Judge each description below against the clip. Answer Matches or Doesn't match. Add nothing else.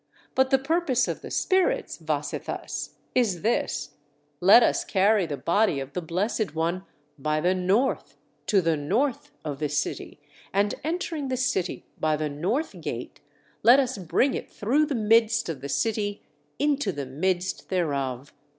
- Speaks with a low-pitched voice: Doesn't match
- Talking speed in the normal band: Matches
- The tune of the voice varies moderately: Doesn't match